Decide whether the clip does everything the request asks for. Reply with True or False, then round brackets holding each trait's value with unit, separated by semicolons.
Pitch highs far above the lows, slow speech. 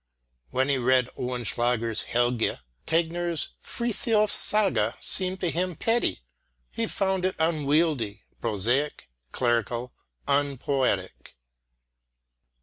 True (6.5 semitones; 90 wpm)